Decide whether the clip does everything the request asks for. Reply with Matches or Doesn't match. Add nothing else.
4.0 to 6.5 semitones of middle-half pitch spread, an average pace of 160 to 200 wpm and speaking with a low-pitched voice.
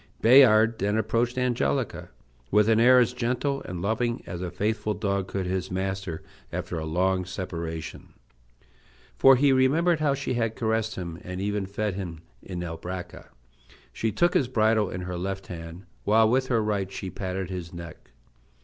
Matches